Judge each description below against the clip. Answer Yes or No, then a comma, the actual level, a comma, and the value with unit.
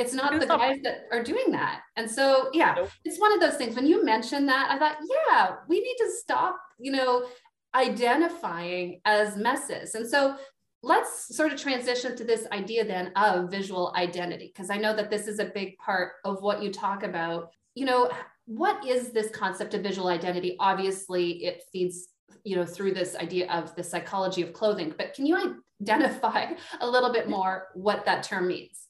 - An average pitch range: No, wide, 6.2 semitones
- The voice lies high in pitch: Yes, high, 215 Hz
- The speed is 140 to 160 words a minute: No, average, 195 wpm